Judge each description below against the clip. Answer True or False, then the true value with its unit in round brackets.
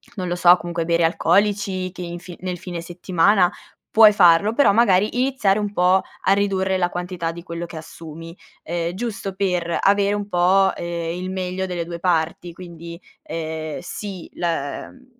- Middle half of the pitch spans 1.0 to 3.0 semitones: True (2.4 semitones)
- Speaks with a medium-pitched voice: True (180 Hz)